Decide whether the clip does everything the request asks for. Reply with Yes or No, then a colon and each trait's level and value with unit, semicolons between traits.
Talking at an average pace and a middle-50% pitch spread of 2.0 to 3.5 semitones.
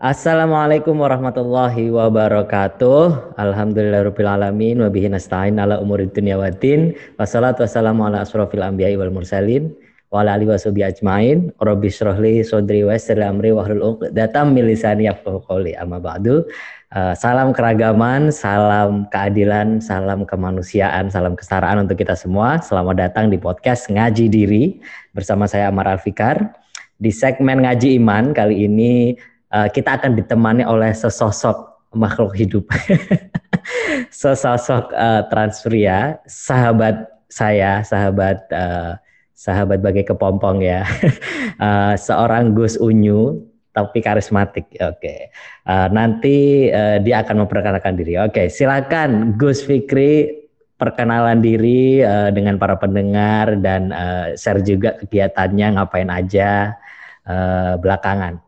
Yes: average, 110 wpm; average, 3.1 semitones